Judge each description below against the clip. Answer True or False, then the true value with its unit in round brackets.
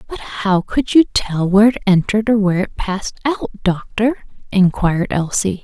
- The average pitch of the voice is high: True (205 Hz)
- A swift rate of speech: False (170 wpm)